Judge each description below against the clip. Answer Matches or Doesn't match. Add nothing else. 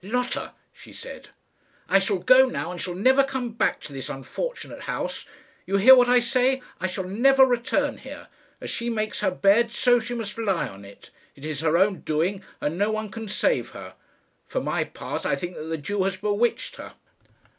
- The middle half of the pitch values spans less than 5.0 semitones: Doesn't match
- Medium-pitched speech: Doesn't match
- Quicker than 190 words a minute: Matches